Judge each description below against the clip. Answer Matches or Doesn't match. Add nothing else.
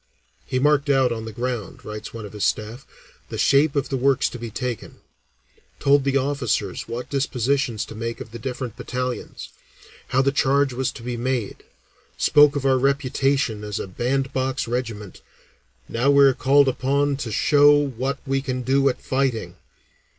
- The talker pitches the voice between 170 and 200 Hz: Doesn't match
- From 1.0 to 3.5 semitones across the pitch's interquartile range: Matches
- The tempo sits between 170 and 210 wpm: Matches